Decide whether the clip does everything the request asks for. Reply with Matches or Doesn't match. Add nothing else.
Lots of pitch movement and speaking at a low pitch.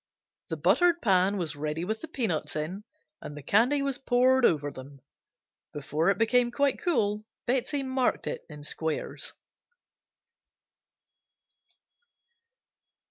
Doesn't match